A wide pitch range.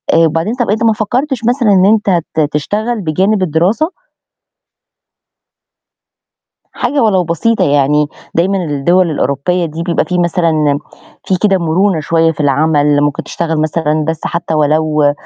No: average, 4.8 semitones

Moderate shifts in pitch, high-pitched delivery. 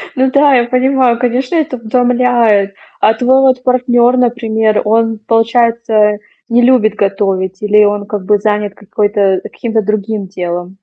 Yes: average, 3.2 semitones; high, 225 Hz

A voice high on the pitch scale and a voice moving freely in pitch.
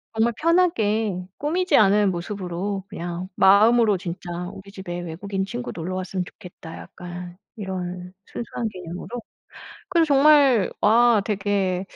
No: high, 195 Hz; average, 4.3 semitones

